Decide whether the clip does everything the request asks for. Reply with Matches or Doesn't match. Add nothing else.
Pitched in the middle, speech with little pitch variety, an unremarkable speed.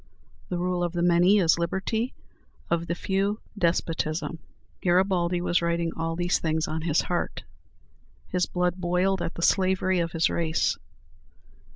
Matches